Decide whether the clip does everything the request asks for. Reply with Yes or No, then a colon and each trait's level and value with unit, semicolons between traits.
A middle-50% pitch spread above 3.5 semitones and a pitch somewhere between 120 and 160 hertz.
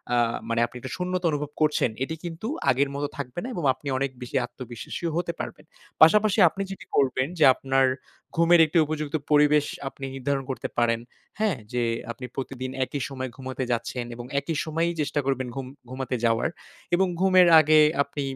Yes: average, 3.9 semitones; medium, 140 Hz